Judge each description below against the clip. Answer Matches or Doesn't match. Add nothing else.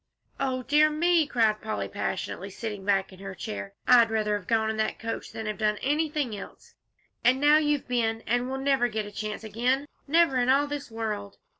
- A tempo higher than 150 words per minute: Matches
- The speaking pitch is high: Matches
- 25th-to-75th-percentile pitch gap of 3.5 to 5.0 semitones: Matches